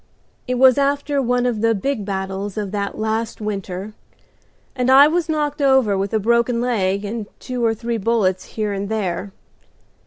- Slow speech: No, average, 175 wpm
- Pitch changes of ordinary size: Yes, average, 3.9 semitones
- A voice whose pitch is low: No, high, 225 Hz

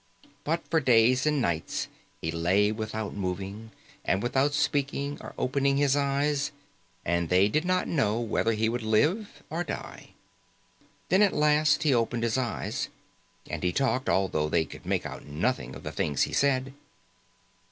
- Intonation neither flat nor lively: No, wide, 6.1 semitones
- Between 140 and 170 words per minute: Yes, average, 165 wpm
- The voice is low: Yes, low, 125 Hz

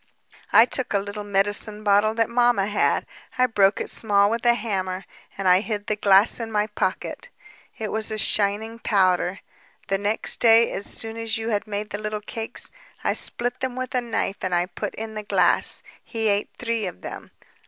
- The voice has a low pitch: No, high, 210 Hz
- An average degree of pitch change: No, narrow, 2.1 semitones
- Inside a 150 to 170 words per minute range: No, average, 195 wpm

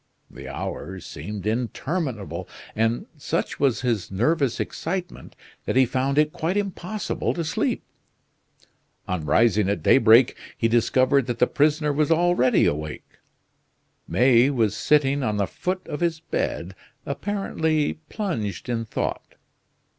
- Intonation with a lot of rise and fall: Yes, wide, 5.9 semitones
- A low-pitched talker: Yes, low, 130 Hz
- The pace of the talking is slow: Yes, slow, 130 wpm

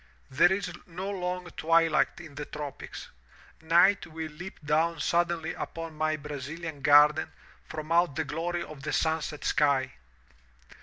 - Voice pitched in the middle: Yes, medium, 160 Hz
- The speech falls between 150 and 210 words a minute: No, average, 140 wpm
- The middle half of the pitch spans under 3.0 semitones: Yes, narrow, 2.4 semitones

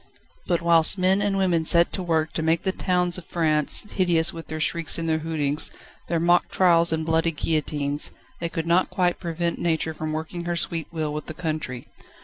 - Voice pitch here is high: No, medium, 165 Hz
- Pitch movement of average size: No, narrow, 1.7 semitones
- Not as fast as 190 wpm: No, average, 200 wpm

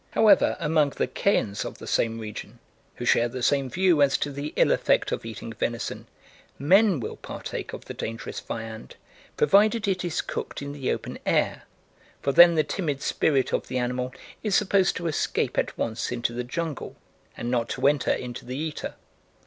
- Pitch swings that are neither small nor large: No, wide, 5.8 semitones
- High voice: No, medium, 140 Hz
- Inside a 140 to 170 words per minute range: No, average, 185 wpm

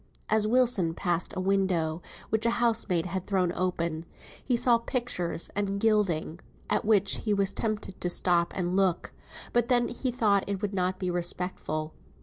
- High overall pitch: Yes, high, 195 Hz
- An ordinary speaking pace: Yes, average, 165 wpm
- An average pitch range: Yes, average, 3.8 semitones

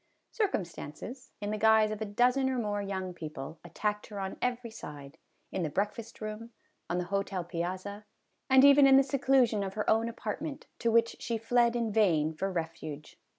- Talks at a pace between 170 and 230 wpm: Yes, average, 185 wpm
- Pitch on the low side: No, high, 210 Hz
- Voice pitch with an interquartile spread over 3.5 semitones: Yes, average, 4.2 semitones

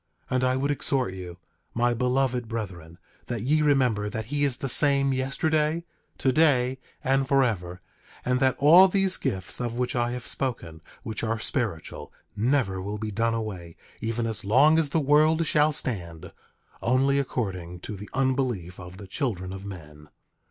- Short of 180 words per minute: Yes, average, 165 wpm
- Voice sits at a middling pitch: No, low, 125 Hz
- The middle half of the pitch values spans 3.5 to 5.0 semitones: No, wide, 5.6 semitones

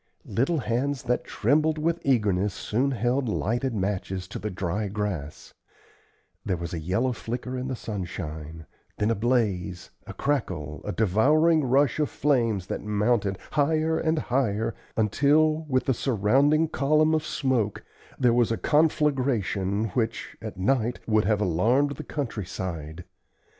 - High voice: No, low, 115 Hz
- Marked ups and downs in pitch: Yes, wide, 5.9 semitones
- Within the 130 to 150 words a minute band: Yes, average, 145 wpm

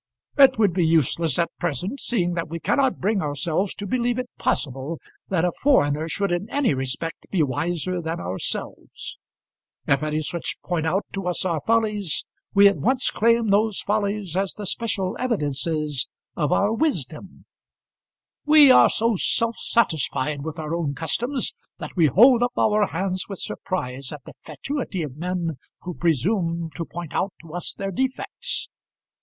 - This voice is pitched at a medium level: Yes, medium, 180 Hz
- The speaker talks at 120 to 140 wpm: No, average, 165 wpm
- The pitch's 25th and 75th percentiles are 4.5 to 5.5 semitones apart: Yes, average, 5.1 semitones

